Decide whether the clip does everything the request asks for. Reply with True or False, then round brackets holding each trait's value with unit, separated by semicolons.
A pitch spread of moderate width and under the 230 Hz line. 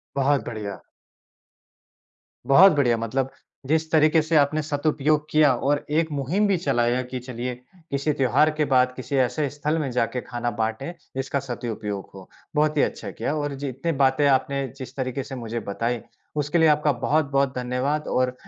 True (3.1 semitones; 135 Hz)